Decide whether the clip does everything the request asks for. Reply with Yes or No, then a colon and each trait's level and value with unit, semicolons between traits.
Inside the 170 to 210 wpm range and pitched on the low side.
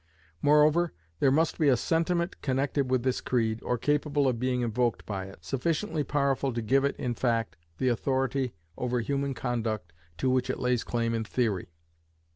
Yes: average, 175 wpm; low, 130 Hz